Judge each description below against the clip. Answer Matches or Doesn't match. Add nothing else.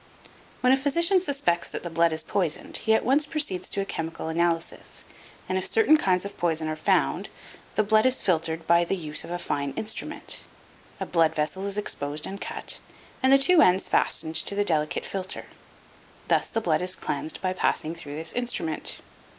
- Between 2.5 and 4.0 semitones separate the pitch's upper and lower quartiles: Doesn't match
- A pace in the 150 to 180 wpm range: Doesn't match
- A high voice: Doesn't match